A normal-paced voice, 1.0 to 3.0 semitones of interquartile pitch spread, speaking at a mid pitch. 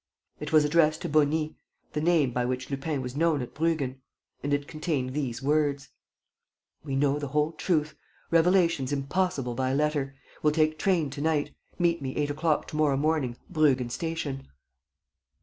Yes: average, 165 wpm; narrow, 2.6 semitones; medium, 150 Hz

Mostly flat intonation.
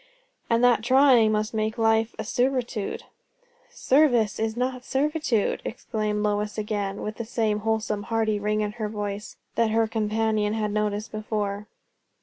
Yes: narrow, 1.7 semitones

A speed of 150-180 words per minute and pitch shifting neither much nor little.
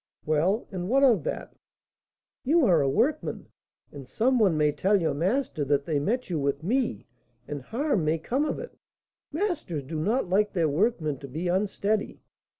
No: average, 175 wpm; wide, 8.1 semitones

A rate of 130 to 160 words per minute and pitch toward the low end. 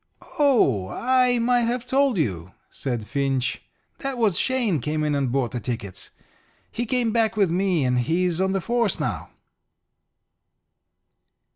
No: average, 145 wpm; medium, 185 Hz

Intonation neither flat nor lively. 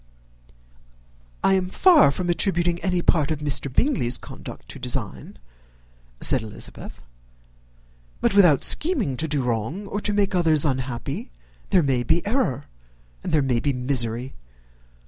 No: wide, 6.5 semitones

